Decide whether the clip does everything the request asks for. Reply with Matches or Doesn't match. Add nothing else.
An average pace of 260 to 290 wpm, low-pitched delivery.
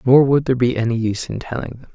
Matches